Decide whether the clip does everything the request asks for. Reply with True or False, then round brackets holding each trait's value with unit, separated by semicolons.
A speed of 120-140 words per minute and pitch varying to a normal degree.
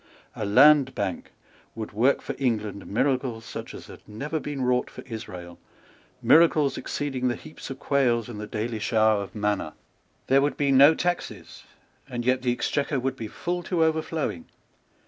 False (165 wpm; 4.7 semitones)